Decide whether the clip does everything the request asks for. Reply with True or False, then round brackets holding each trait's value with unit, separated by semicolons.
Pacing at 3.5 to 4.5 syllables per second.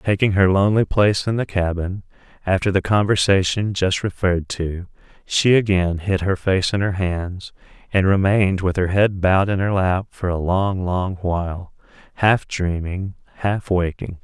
False (4.7 syllables/s)